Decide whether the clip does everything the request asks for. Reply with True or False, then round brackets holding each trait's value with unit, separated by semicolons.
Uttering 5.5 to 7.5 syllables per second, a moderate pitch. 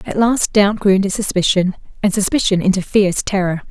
False (5.9 syllables/s; 195 Hz)